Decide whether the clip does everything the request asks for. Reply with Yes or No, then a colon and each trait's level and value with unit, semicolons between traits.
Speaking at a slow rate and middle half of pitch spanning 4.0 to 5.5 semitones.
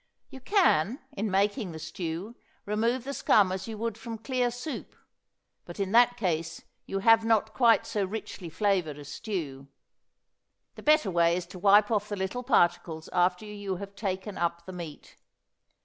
No: average, 170 wpm; average, 4.5 semitones